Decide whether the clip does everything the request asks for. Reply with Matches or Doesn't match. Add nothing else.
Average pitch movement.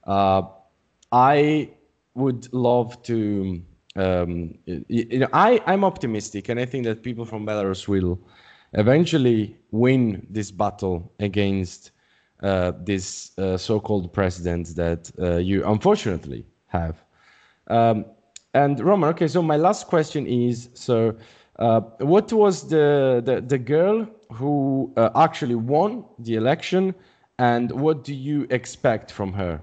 Doesn't match